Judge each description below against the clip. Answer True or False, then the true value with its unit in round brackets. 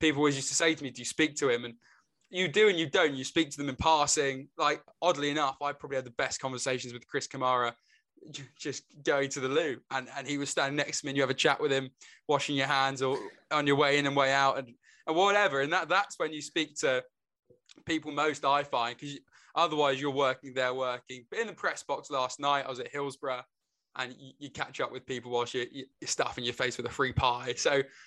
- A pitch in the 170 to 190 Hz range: False (140 Hz)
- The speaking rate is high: True (250 wpm)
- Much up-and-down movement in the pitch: False (2.4 semitones)